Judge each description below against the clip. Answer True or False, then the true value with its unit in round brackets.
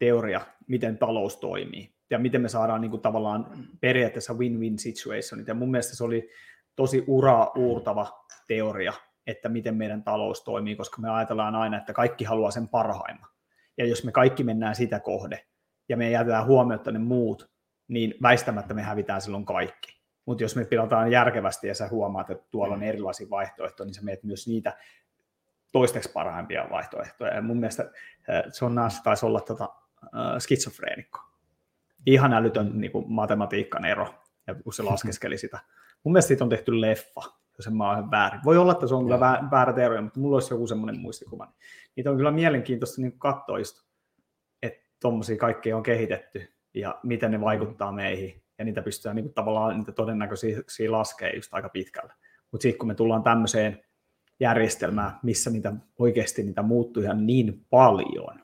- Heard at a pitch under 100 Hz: False (115 Hz)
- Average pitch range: False (2.2 semitones)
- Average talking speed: False (170 wpm)